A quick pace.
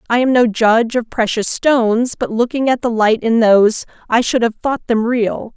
Yes: fast, 215 wpm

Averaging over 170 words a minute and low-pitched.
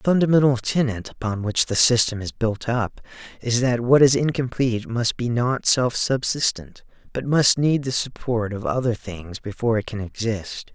Yes: average, 180 wpm; low, 120 Hz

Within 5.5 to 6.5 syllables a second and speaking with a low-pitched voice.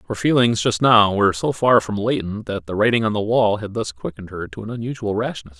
Yes: 6.0 syllables/s; low, 105 Hz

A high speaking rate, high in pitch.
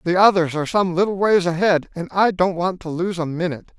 No: fast, 240 wpm; medium, 175 Hz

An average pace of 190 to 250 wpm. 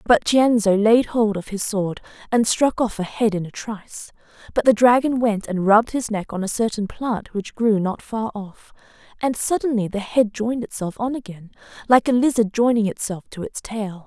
Yes: fast, 205 wpm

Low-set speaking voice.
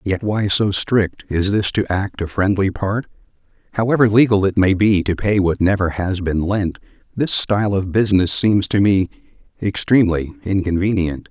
Yes: low, 100 Hz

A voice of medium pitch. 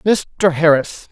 Yes: medium, 170 Hz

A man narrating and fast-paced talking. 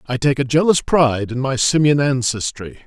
No: male; average, 190 wpm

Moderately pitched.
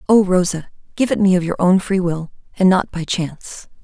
Yes: medium, 180 Hz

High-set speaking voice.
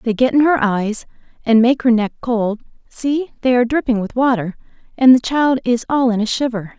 Yes: high, 240 Hz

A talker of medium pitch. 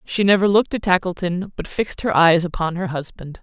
Yes: medium, 180 Hz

